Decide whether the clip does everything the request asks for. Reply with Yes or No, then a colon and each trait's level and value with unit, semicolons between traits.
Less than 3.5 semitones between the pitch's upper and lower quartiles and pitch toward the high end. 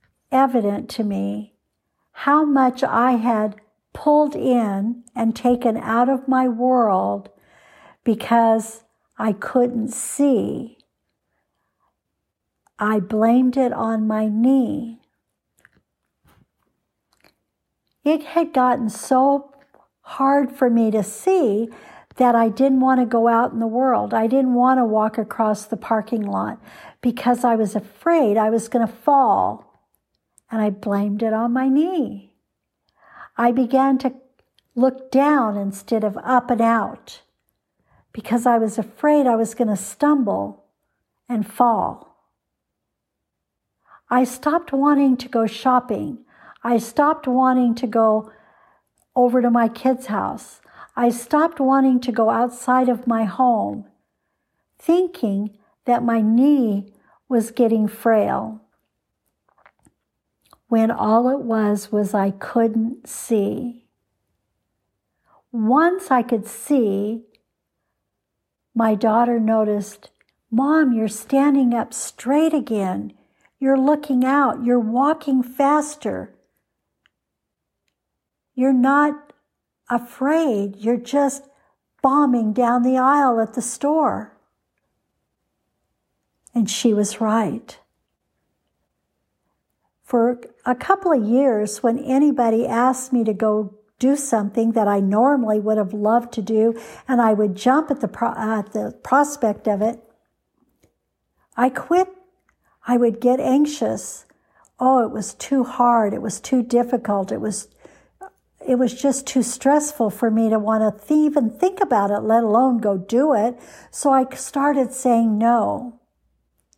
Yes: average, 3.1 semitones; high, 240 Hz